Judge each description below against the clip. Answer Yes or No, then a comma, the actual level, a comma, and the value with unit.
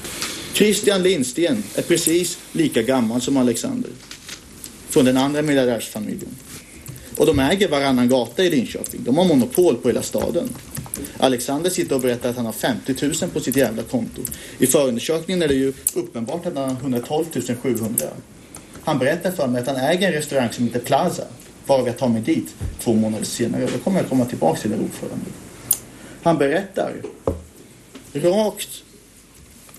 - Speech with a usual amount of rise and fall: Yes, average, 5.0 semitones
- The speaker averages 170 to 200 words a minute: No, average, 160 wpm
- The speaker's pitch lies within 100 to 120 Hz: No, low, 135 Hz